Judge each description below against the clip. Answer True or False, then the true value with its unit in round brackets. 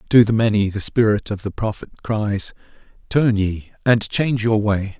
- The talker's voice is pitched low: True (105 Hz)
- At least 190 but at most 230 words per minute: False (180 wpm)